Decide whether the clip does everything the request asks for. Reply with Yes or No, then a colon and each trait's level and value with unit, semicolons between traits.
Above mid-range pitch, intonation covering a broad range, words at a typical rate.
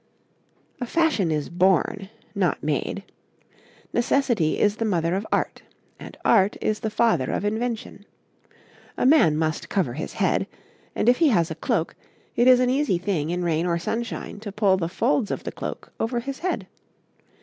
Yes: high, 205 Hz; wide, 5.7 semitones; average, 170 wpm